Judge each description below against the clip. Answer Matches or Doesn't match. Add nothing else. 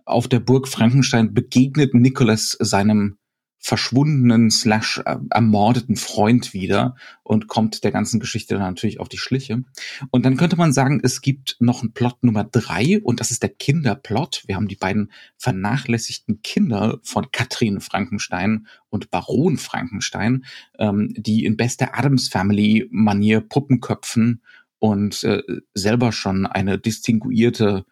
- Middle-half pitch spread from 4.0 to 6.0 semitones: Doesn't match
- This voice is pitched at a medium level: Doesn't match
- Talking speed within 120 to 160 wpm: Matches